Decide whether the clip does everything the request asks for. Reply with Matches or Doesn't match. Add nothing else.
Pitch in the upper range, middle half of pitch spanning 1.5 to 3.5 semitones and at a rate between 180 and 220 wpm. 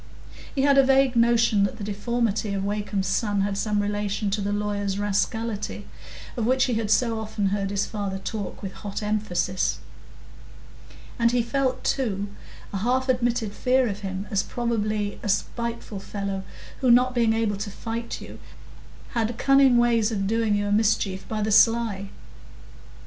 Doesn't match